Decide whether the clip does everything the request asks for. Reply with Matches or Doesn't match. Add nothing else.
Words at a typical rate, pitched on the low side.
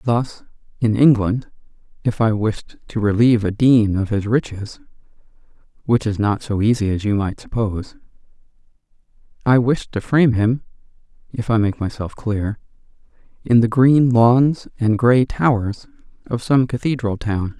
Matches